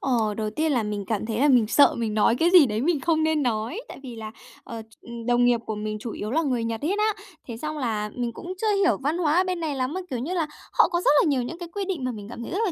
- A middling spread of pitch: No, wide, 6.6 semitones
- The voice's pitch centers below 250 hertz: No, very high, 255 Hz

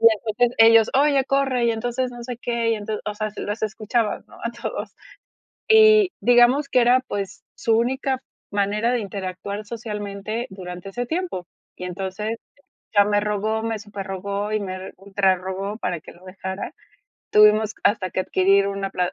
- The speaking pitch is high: Yes, high, 210 Hz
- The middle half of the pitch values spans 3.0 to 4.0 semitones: Yes, average, 3.3 semitones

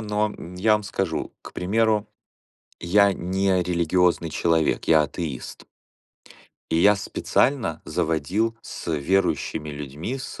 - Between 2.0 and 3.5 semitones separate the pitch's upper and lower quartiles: No, average, 4.3 semitones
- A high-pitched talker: No, very low, 90 Hz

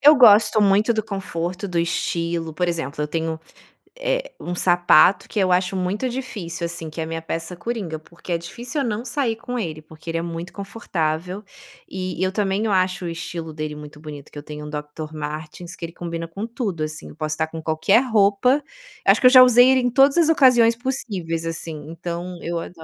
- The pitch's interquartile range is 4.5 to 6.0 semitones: Yes, average, 5.3 semitones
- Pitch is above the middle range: No, medium, 175 Hz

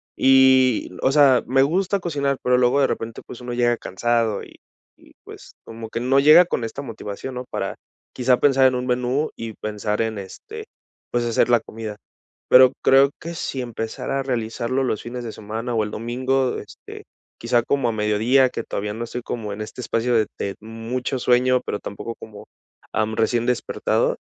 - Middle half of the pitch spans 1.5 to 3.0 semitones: Yes, average, 2.7 semitones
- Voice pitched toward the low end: Yes, low, 120 Hz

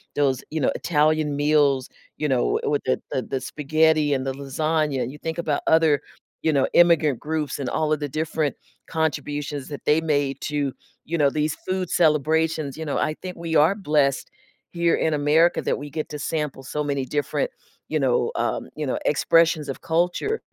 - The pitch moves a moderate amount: No, narrow, 2.1 semitones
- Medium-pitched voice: Yes, medium, 150 Hz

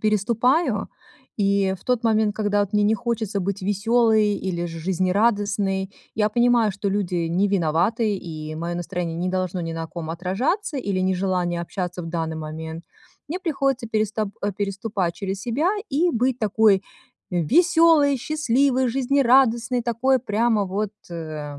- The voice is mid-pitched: No, high, 205 Hz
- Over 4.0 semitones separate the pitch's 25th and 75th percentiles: Yes, average, 4.6 semitones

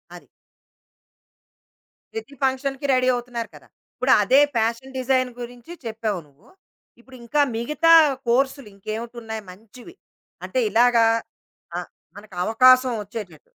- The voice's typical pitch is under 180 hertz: No, high, 240 Hz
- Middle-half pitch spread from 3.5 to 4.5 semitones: No, average, 2.9 semitones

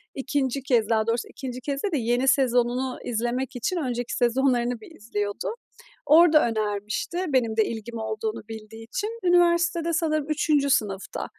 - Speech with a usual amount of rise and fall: Yes, average, 4.8 semitones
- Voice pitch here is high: Yes, very high, 250 Hz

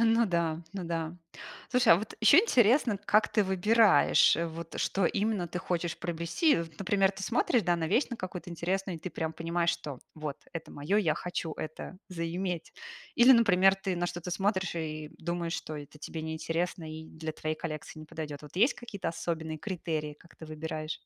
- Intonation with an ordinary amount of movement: Yes, average, 3.5 semitones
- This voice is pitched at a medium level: Yes, medium, 170 Hz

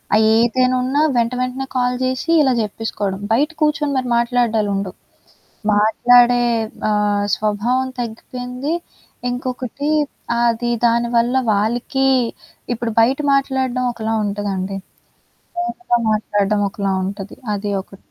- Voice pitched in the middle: No, high, 235 Hz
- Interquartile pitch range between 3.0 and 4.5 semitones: Yes, average, 3.5 semitones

